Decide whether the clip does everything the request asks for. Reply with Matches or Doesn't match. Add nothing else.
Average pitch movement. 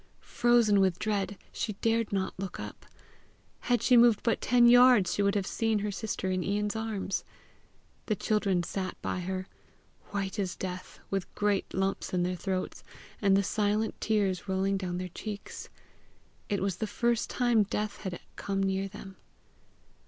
Doesn't match